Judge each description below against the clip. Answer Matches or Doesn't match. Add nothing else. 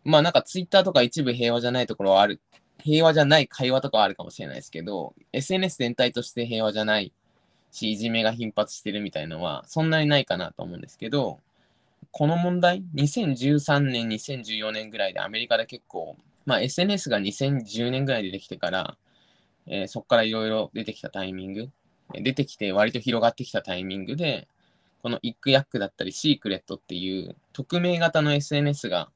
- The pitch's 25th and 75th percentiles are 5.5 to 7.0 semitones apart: Doesn't match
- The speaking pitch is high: Doesn't match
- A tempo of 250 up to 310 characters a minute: Doesn't match